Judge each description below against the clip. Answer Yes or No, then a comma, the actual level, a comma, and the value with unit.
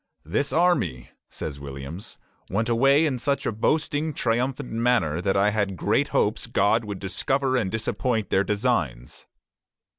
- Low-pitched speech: Yes, low, 110 Hz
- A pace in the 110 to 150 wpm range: Yes, average, 145 wpm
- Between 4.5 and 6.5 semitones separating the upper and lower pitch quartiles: Yes, wide, 5.4 semitones